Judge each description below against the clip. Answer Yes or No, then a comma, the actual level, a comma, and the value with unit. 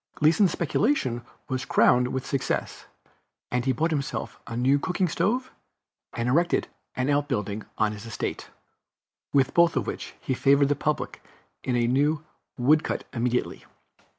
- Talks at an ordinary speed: Yes, average, 150 wpm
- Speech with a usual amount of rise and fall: Yes, average, 3.8 semitones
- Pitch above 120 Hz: Yes, low, 135 Hz